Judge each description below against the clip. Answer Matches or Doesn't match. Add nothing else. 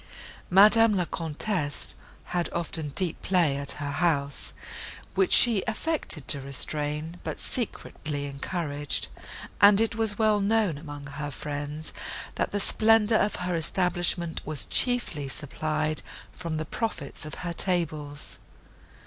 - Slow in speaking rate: Matches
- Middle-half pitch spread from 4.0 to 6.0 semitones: Matches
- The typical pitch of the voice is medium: Matches